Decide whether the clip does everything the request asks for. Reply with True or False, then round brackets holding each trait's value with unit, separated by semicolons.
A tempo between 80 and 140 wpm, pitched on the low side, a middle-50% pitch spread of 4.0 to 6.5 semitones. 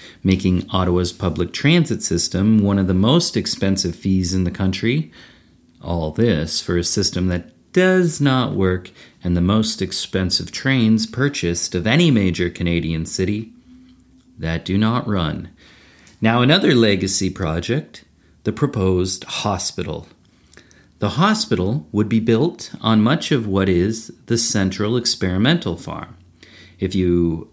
True (135 wpm; 95 Hz; 4.7 semitones)